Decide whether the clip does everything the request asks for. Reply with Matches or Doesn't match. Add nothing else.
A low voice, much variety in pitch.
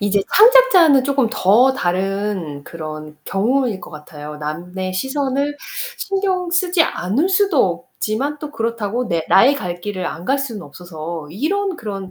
Doesn't match